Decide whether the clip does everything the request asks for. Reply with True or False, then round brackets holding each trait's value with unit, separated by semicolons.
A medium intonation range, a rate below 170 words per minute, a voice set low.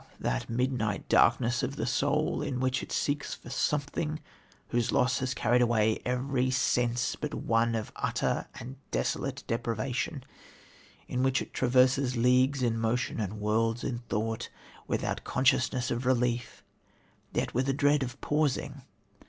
False (2.3 semitones; 145 wpm; 125 Hz)